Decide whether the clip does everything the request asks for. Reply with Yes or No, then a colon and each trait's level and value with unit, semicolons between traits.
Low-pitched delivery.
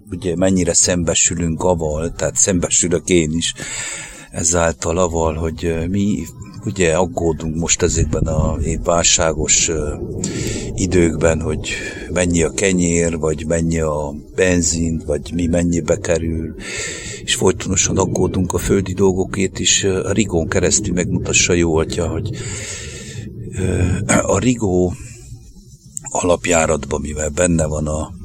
Yes: very low, 85 Hz